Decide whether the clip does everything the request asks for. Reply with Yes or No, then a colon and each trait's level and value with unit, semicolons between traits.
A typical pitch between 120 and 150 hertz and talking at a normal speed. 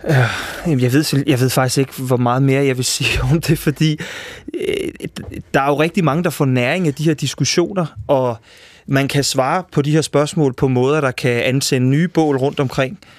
Yes: medium, 140 Hz; average, 200 wpm